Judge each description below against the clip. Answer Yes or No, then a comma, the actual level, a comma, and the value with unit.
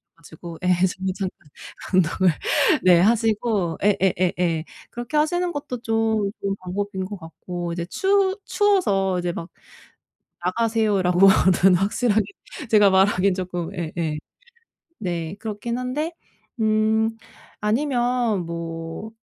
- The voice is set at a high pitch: Yes, high, 195 Hz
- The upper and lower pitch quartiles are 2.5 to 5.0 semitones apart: Yes, average, 4.1 semitones